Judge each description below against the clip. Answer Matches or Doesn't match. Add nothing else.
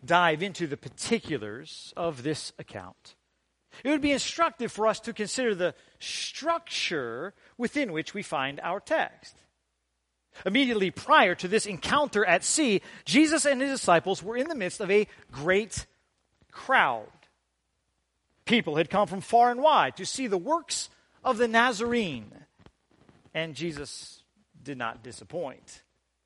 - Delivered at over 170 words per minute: Doesn't match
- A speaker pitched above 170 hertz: Matches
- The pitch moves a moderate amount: Doesn't match